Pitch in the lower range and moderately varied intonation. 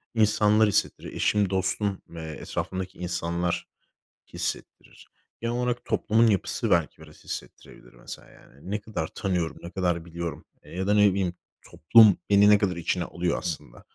Yes: very low, 95 Hz; average, 3.4 semitones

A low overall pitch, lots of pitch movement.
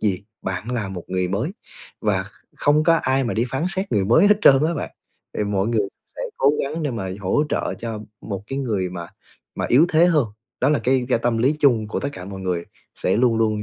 Yes: low, 115 Hz; wide, 5.9 semitones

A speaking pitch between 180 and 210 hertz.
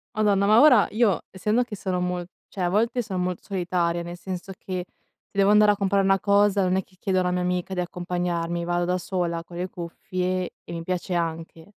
Yes: medium, 185 Hz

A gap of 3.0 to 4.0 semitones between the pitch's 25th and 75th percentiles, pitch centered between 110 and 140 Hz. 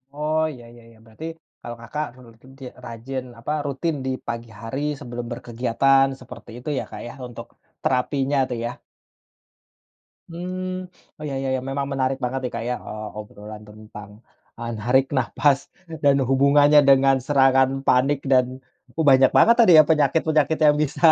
Yes: average, 3.5 semitones; low, 135 Hz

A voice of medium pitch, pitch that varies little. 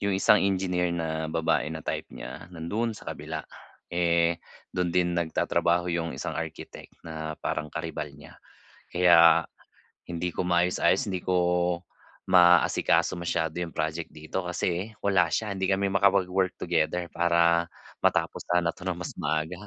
No: very low, 85 Hz; narrow, 1.9 semitones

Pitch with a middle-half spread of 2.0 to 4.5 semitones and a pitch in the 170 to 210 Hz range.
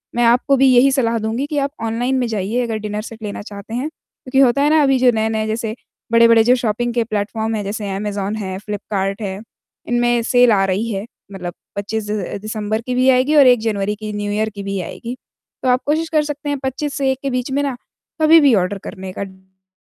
No: average, 3.8 semitones; high, 225 Hz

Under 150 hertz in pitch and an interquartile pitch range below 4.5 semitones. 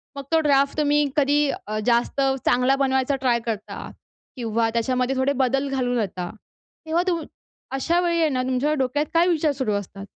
No: very high, 270 Hz; average, 3.1 semitones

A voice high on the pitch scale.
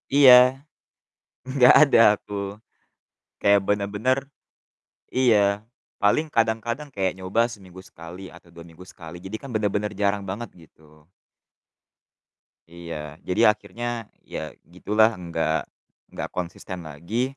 No: low, 100 Hz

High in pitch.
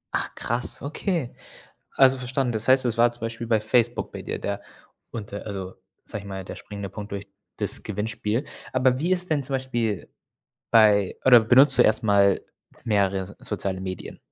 No: low, 115 Hz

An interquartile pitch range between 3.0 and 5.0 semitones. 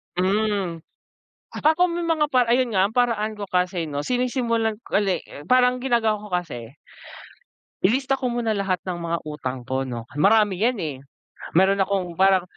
No: wide, 5.4 semitones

